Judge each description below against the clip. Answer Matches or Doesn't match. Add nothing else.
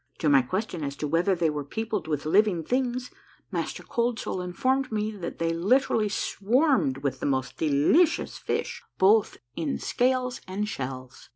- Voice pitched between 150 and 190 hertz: Matches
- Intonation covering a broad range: Matches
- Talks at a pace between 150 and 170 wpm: Matches